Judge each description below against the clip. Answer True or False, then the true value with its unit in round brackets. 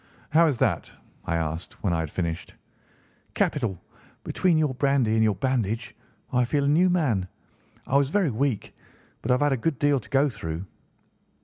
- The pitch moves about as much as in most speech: False (6.6 semitones)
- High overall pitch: False (125 Hz)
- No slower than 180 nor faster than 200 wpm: True (185 wpm)